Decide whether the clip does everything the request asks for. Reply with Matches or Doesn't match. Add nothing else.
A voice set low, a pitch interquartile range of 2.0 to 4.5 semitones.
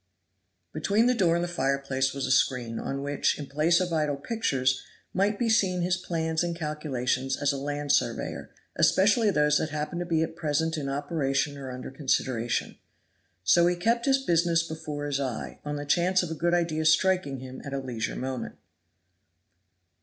Doesn't match